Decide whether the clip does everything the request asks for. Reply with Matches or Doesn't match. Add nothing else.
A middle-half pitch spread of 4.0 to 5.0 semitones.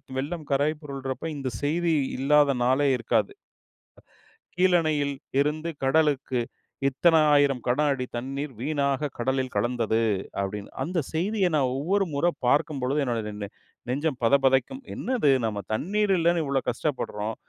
Doesn't match